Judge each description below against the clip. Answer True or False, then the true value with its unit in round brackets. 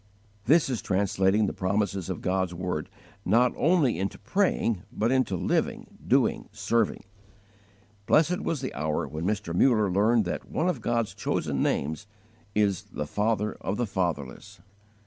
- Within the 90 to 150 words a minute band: True (145 wpm)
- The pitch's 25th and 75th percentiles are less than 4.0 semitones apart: False (4.3 semitones)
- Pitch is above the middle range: False (105 Hz)